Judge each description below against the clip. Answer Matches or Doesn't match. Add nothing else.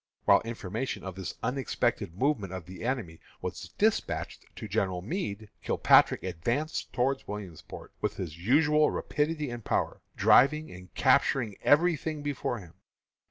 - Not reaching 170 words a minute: Matches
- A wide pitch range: Matches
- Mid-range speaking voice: Doesn't match